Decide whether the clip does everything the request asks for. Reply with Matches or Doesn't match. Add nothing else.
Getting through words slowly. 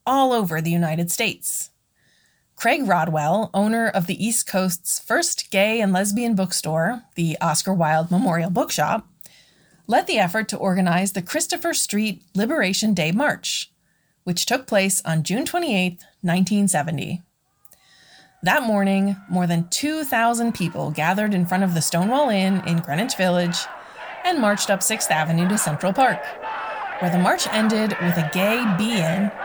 Doesn't match